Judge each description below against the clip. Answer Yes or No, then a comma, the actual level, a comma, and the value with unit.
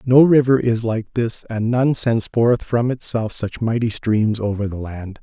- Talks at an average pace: Yes, average, 195 wpm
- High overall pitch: No, low, 115 Hz